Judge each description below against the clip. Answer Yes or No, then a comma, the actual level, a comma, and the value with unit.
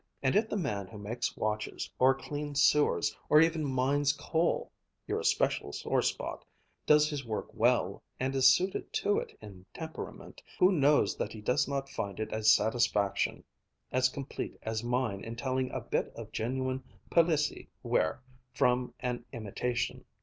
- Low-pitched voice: Yes, low, 130 Hz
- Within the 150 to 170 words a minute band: Yes, average, 160 wpm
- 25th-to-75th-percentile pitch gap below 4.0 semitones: No, average, 4.5 semitones